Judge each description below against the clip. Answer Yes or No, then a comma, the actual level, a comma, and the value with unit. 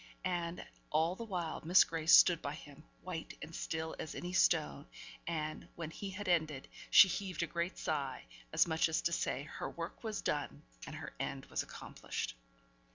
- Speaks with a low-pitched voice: No, medium, 165 Hz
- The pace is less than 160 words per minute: No, average, 180 wpm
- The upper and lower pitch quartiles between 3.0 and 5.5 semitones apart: No, narrow, 2.5 semitones